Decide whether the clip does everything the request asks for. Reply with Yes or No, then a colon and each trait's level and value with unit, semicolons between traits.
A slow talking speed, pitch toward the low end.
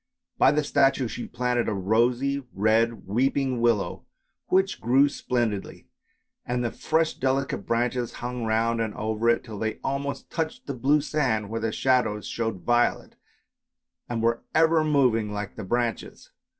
No: average, 150 wpm; low, 120 Hz